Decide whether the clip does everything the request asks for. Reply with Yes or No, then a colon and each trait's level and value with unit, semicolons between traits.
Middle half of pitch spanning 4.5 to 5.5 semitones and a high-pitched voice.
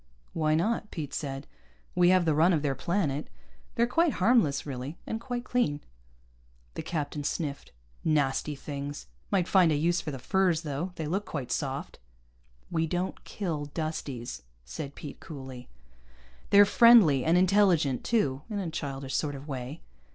No: average, 4.8 semitones; medium, 155 Hz